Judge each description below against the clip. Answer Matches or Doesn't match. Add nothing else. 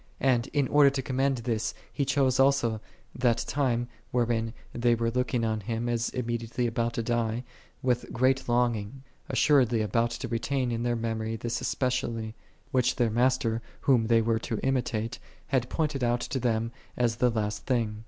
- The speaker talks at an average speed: Matches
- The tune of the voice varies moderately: Doesn't match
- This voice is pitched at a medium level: Doesn't match